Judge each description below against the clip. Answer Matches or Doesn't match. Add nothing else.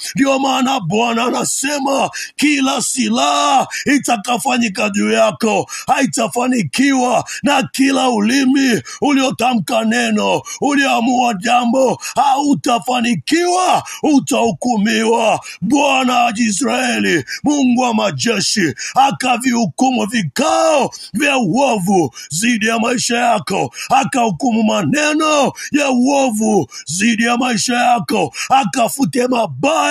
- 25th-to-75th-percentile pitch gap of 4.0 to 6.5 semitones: Doesn't match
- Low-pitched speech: Doesn't match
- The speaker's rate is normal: Doesn't match